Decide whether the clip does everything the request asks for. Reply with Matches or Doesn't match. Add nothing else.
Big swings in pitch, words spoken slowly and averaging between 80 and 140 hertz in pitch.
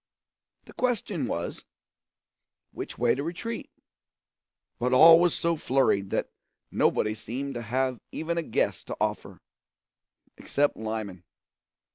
Matches